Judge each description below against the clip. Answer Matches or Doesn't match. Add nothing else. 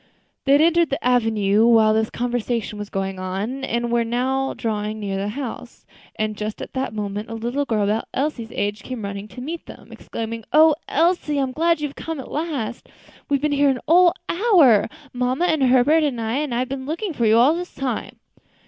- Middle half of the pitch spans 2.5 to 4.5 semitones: Doesn't match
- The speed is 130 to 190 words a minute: Doesn't match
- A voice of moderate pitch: Doesn't match